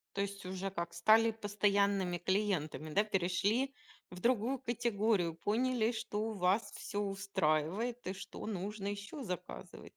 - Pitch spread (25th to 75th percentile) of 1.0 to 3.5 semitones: Yes, average, 3.1 semitones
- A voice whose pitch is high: Yes, high, 200 Hz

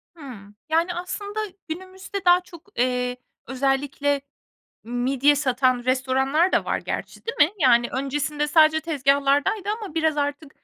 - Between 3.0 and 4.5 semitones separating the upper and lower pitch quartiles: Yes, average, 4.1 semitones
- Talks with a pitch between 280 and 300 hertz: Yes, very high, 285 Hz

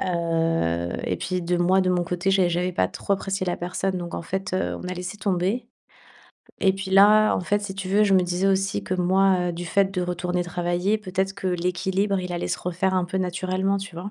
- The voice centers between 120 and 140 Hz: No, medium, 185 Hz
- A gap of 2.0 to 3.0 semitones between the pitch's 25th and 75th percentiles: No, narrow, 1.5 semitones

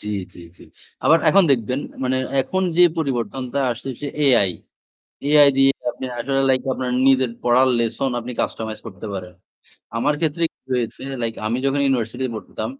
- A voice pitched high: No, low, 130 Hz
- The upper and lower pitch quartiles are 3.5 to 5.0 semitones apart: No, average, 2.9 semitones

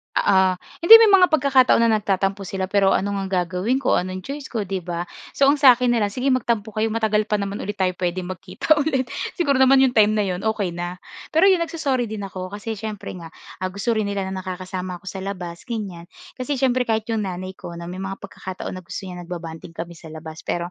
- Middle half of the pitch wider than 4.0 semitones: Yes, average, 4.8 semitones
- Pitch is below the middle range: No, high, 200 Hz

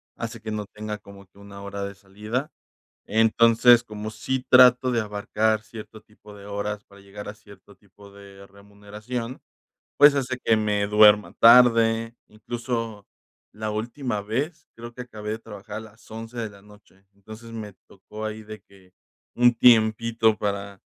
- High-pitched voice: No, low, 110 Hz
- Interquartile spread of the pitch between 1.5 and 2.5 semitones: Yes, narrow, 2.1 semitones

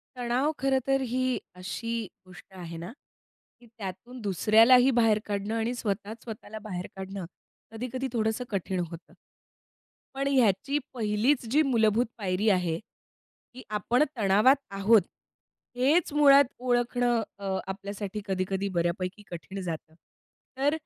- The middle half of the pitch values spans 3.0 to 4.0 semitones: No, average, 4.4 semitones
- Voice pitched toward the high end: Yes, high, 220 Hz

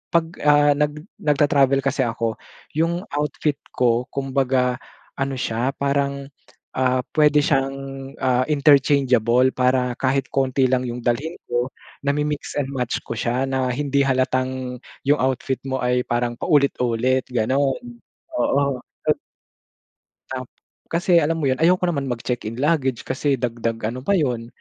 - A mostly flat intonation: Yes, narrow, 2.3 semitones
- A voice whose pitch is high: No, low, 135 Hz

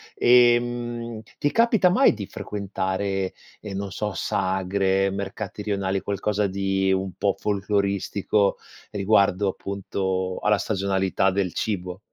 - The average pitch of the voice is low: Yes, low, 100 Hz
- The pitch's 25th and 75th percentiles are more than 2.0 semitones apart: No, narrow, 1.7 semitones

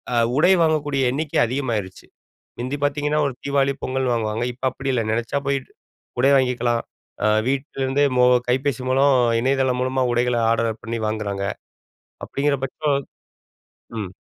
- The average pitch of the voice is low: Yes, low, 130 Hz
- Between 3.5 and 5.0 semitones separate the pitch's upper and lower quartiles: No, average, 2.9 semitones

